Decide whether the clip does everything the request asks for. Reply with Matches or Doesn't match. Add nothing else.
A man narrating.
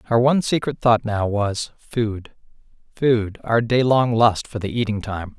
Matches